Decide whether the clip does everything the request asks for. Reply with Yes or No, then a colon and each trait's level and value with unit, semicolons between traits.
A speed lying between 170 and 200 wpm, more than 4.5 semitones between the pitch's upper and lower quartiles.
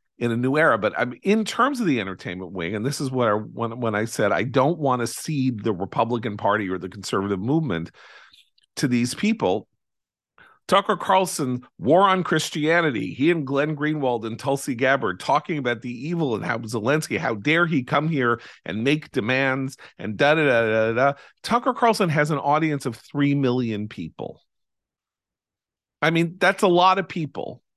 Yes: average, 180 wpm; wide, 5.6 semitones